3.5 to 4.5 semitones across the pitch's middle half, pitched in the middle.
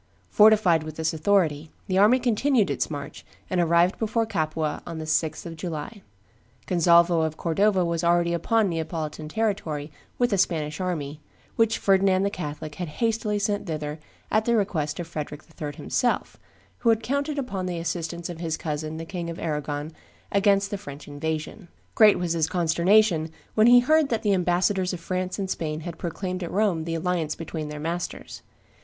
Yes: average, 4.2 semitones; medium, 175 Hz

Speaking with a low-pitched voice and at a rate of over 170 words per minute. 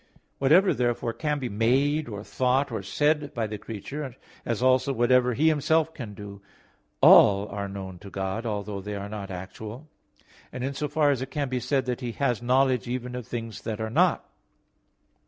Yes: low, 125 Hz; average, 185 wpm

